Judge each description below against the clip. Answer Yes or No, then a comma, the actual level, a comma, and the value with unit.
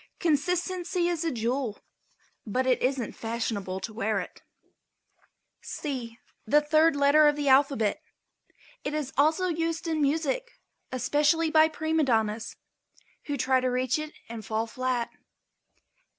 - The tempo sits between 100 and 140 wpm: Yes, slow, 135 wpm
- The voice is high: Yes, very high, 280 Hz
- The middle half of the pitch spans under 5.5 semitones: Yes, average, 5.1 semitones